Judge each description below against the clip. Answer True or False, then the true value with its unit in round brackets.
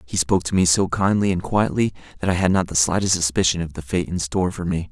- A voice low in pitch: True (90 Hz)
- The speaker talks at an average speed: False (270 wpm)